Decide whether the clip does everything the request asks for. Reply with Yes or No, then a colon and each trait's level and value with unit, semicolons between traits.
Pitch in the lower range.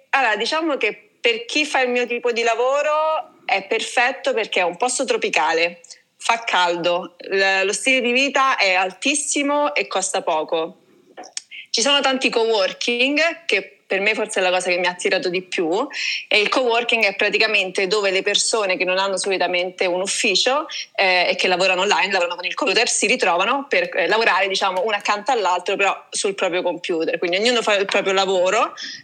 No: high, 210 Hz